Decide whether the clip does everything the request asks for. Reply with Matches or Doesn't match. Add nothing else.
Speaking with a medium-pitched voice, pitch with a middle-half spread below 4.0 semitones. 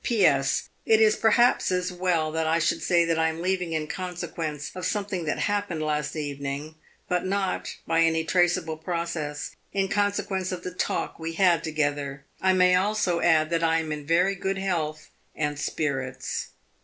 Matches